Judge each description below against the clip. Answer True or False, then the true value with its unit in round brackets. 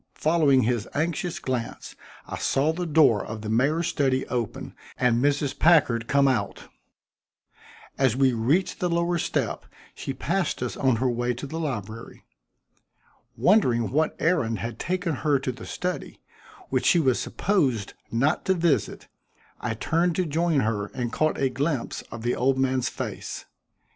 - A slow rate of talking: False (160 wpm)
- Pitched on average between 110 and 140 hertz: True (135 Hz)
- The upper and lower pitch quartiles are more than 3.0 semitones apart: True (5.2 semitones)